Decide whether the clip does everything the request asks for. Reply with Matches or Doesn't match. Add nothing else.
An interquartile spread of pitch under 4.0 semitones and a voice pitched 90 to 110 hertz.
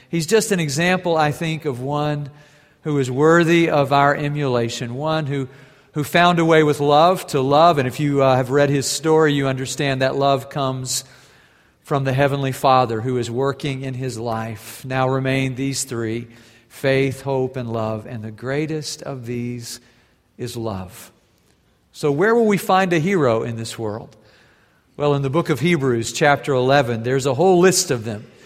Doesn't match